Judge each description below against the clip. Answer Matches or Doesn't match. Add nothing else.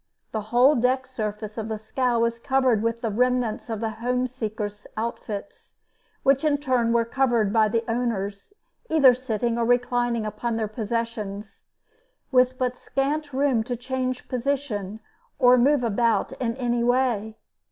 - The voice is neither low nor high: Doesn't match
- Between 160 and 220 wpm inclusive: Doesn't match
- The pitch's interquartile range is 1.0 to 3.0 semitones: Matches